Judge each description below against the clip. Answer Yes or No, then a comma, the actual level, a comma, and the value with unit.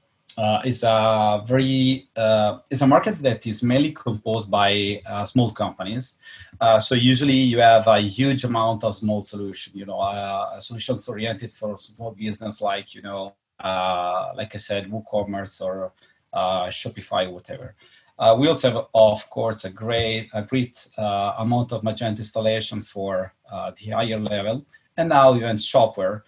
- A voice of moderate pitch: No, low, 110 Hz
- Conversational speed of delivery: Yes, average, 160 wpm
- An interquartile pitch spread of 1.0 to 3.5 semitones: Yes, average, 3.0 semitones